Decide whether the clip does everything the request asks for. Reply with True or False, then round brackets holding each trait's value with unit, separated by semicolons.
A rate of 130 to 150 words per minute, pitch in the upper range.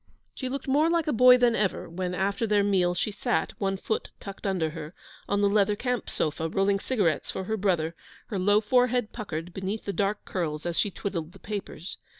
False (205 wpm; 200 Hz)